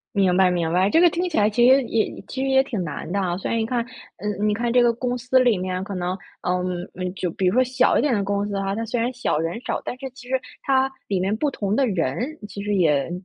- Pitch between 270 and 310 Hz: No, high, 210 Hz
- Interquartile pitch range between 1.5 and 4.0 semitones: No, average, 5.1 semitones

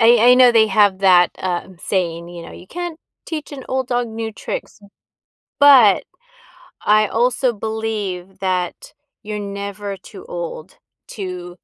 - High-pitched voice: Yes, high, 210 Hz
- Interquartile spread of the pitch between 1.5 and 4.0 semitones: No, average, 4.6 semitones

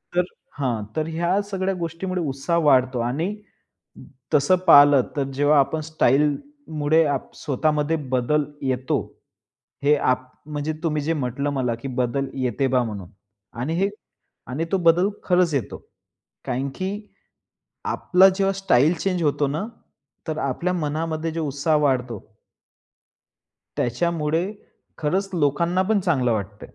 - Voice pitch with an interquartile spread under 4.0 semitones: No, average, 4.3 semitones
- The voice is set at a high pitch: No, medium, 150 Hz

